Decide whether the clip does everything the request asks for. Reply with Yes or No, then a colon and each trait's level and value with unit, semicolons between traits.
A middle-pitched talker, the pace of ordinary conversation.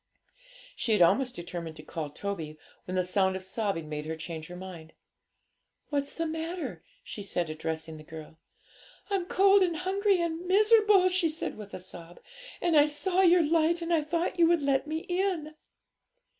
No: very high, 290 Hz; average, 180 wpm